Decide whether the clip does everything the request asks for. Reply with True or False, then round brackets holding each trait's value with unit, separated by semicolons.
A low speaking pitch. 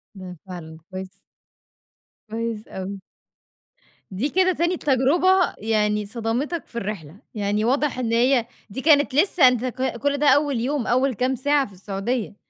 False (240 Hz)